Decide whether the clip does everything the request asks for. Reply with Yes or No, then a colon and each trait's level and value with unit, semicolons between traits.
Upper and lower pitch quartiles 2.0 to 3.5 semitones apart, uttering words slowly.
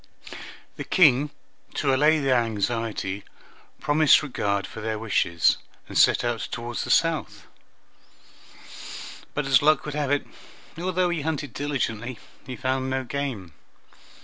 No: average, 4.6 semitones; slow, 130 wpm